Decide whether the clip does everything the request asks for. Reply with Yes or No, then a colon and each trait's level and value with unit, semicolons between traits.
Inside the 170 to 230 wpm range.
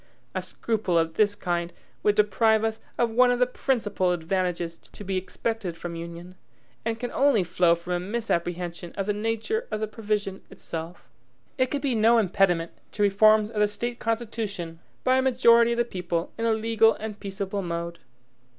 Yes: average, 180 wpm